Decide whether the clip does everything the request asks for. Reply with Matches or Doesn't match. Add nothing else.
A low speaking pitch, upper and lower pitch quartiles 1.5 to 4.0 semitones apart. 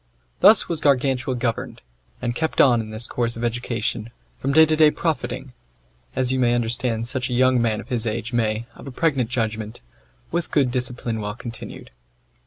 Matches